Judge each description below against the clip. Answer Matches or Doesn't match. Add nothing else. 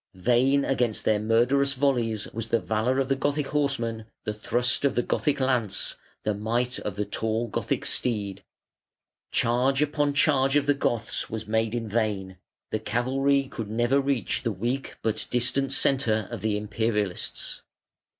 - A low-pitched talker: Matches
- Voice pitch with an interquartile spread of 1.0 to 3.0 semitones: Doesn't match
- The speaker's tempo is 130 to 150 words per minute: Doesn't match